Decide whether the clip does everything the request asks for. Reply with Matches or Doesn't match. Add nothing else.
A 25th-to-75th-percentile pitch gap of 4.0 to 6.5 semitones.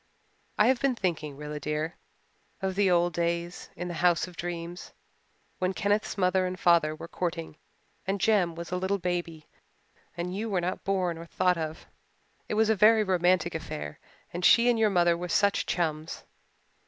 Doesn't match